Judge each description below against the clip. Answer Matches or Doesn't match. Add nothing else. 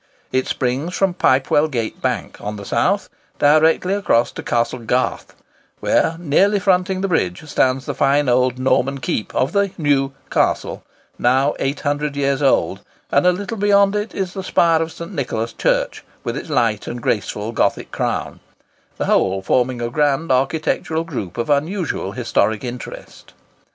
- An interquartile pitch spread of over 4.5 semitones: Matches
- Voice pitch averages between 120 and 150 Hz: Matches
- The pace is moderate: Matches